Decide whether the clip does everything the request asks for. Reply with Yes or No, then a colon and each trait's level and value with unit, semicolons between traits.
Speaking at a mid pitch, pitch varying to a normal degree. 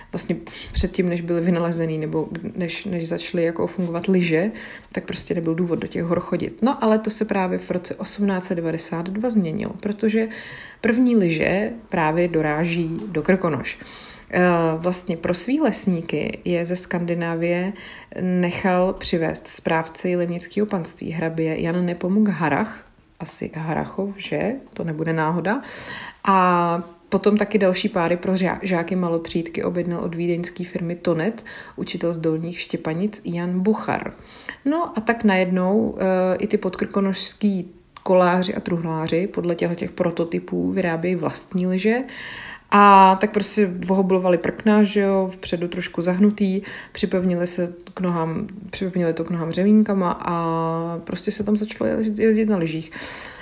Yes: medium, 180 Hz; average, 3.1 semitones